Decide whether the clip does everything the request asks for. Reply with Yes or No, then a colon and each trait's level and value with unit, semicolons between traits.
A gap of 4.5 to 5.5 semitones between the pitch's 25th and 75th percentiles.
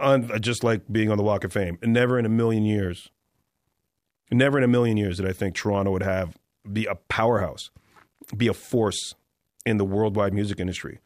No: average, 2.9 semitones